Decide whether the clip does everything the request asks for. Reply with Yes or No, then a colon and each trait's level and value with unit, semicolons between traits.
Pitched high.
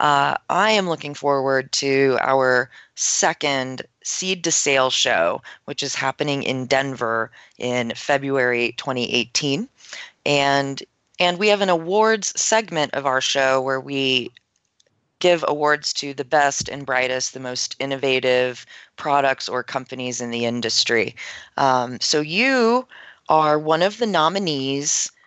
No: medium, 140 Hz